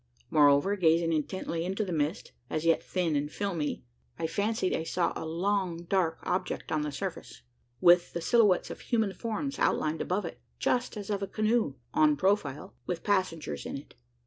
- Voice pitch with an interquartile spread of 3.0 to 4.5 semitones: Yes, average, 4.1 semitones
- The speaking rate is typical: Yes, average, 175 wpm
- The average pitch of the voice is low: No, medium, 175 Hz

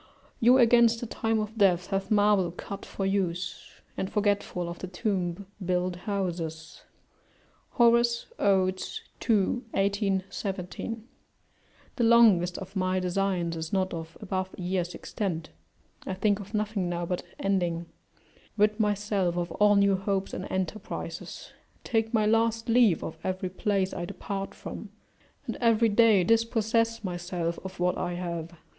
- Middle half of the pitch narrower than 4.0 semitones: Yes, average, 3.1 semitones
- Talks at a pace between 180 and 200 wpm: No, average, 145 wpm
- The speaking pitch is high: Yes, high, 195 Hz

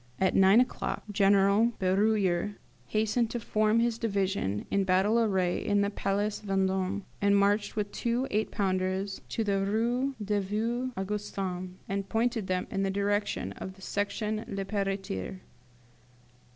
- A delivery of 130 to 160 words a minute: Yes, average, 140 wpm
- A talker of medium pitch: No, high, 200 Hz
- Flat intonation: Yes, narrow, 2.0 semitones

